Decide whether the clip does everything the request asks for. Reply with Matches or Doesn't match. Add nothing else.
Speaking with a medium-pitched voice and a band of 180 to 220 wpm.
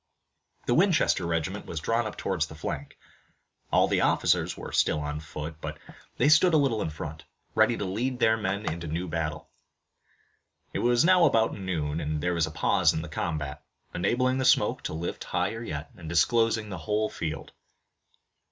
Doesn't match